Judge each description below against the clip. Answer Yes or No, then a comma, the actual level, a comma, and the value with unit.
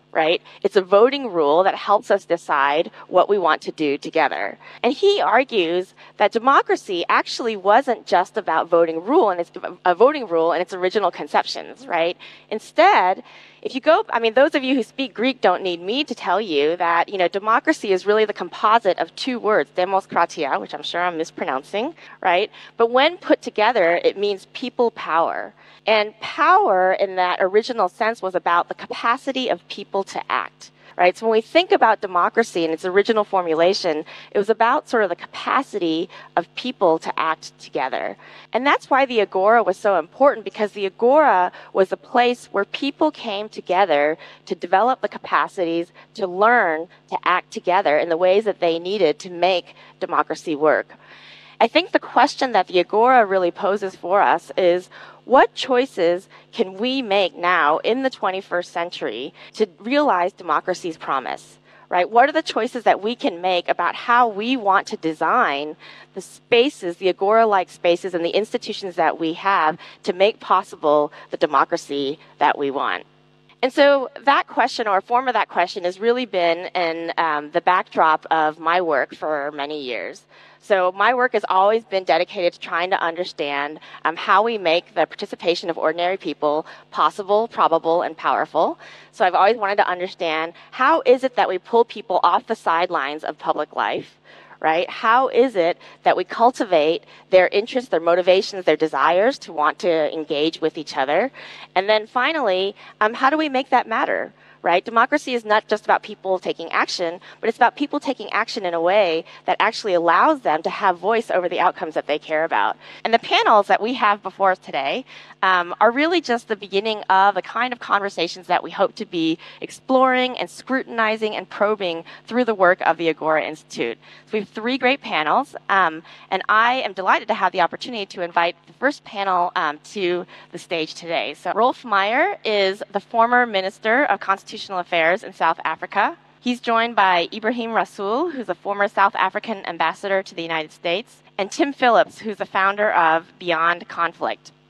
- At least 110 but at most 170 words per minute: No, average, 185 wpm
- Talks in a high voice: Yes, high, 195 Hz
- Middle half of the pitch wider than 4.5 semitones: Yes, average, 5.1 semitones